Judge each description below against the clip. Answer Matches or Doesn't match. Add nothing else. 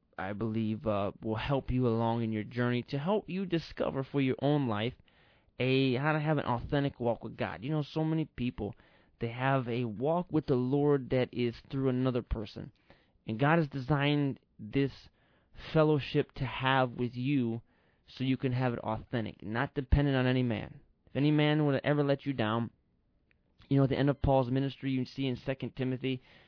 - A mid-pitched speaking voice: Doesn't match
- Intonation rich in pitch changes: Doesn't match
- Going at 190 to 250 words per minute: Matches